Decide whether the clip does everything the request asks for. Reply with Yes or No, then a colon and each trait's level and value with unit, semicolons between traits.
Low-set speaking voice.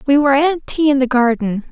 No: very high, 270 Hz